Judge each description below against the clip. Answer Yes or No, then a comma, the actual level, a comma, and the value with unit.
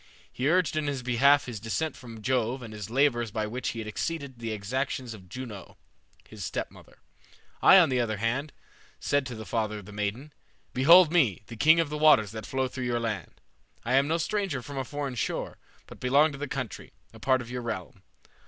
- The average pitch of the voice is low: Yes, low, 125 Hz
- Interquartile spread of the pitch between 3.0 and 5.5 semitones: Yes, average, 4.2 semitones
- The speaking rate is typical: No, fast, 210 wpm